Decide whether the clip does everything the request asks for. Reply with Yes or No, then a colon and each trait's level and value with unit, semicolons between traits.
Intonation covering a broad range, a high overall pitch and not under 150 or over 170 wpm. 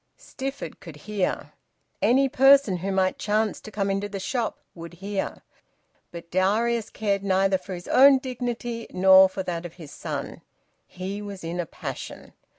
No: average, 3.8 semitones; high, 195 Hz; average, 160 wpm